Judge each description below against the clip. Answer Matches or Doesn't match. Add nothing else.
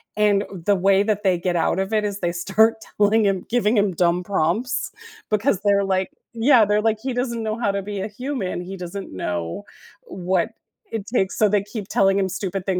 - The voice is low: Doesn't match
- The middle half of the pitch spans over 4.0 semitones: Doesn't match